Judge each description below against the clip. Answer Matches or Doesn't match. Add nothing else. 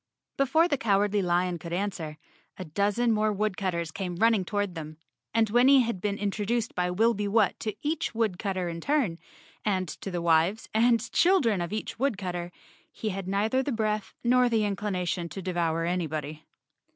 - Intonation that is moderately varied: Matches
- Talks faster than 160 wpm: Matches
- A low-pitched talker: Doesn't match